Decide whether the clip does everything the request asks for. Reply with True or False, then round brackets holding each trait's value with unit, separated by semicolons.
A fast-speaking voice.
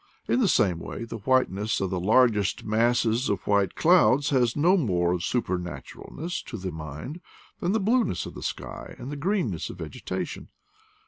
False (180 wpm)